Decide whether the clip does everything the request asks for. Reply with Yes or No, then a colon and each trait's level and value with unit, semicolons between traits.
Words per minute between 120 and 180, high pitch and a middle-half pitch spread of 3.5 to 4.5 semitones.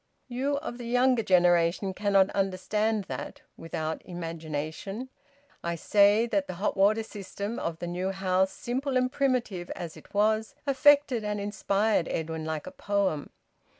No: average, 150 wpm; high, 200 Hz; average, 5.0 semitones